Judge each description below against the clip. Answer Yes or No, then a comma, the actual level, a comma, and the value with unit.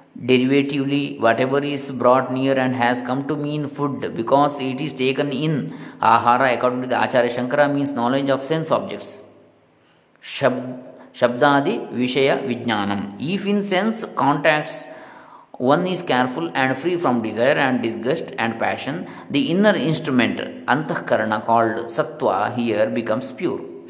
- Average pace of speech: No, fast, 140 wpm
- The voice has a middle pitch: No, low, 130 Hz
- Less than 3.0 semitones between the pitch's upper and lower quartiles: Yes, narrow, 2.6 semitones